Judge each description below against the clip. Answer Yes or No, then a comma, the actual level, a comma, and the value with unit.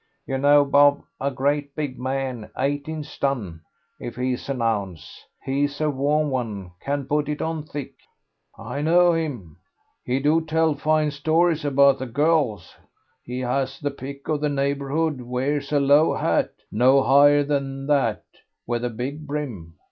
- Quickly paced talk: No, average, 155 wpm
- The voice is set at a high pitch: No, medium, 140 Hz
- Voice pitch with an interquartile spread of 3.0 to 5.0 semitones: No, narrow, 2.4 semitones